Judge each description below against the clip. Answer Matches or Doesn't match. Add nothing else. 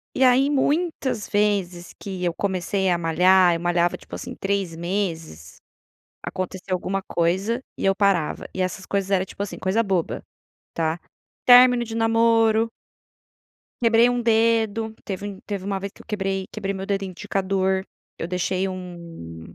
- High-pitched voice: Matches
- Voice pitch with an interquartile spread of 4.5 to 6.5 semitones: Doesn't match